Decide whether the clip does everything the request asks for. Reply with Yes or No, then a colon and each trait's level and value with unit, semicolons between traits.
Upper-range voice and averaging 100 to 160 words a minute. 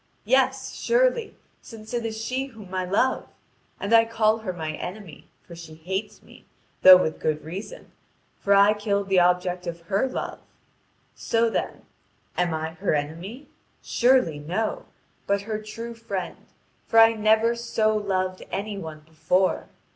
Yes: high, 200 Hz; average, 155 wpm